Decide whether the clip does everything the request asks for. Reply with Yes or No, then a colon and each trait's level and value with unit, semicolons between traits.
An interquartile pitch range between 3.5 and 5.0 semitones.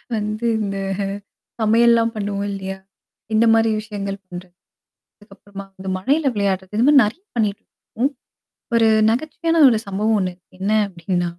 No: average, 2.8 semitones